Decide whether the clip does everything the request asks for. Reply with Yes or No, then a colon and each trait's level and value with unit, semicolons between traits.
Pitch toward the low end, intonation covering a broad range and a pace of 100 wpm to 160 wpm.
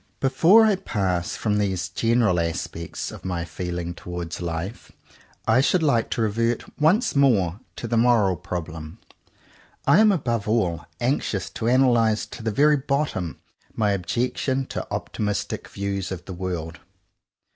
Yes: low, 105 Hz; wide, 5.8 semitones; average, 145 wpm